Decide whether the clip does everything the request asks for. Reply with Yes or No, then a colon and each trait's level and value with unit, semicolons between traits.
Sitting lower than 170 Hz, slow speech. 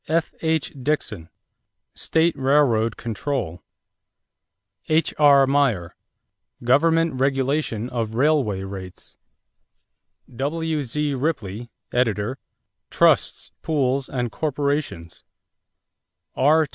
Yes: low, 135 Hz; slow, 70 wpm